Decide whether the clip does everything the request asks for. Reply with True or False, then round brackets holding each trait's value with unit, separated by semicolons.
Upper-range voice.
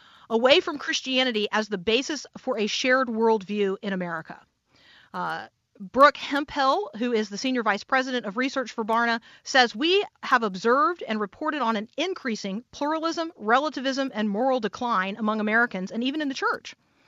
True (245 Hz)